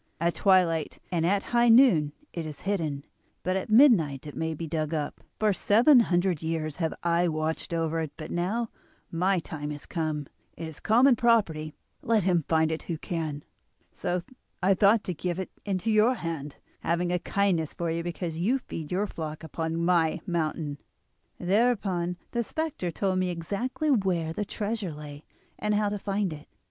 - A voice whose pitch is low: No, medium, 175 Hz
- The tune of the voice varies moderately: Yes, average, 4.1 semitones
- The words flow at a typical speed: Yes, average, 180 wpm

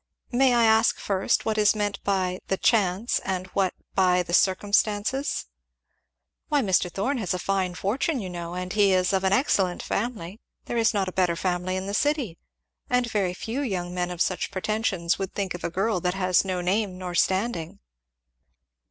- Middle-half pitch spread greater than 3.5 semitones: No, average, 3.2 semitones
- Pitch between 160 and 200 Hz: Yes, high, 190 Hz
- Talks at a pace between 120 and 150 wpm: No, average, 185 wpm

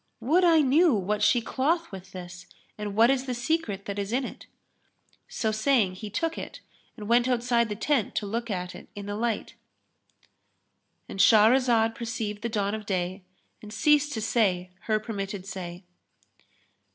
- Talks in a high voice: Yes, high, 220 Hz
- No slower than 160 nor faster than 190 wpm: Yes, average, 165 wpm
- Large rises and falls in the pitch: No, average, 3.7 semitones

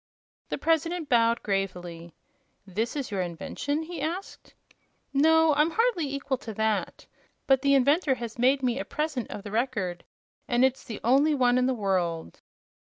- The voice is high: Yes, very high, 255 Hz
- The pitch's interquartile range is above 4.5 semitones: Yes, wide, 5.6 semitones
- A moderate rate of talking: Yes, average, 165 wpm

